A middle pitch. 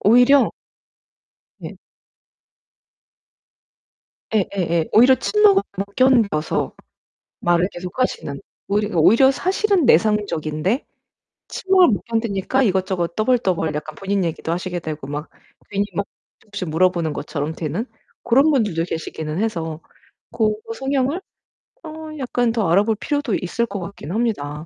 No: high, 200 Hz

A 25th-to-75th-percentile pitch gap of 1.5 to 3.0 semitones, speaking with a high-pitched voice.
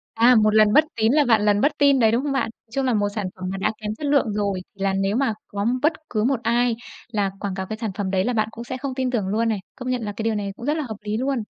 No: average, 3.7 semitones; high, 225 Hz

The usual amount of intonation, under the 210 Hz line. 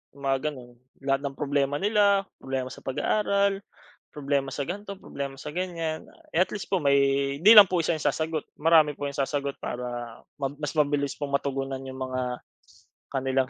Yes: average, 3.2 semitones; medium, 140 Hz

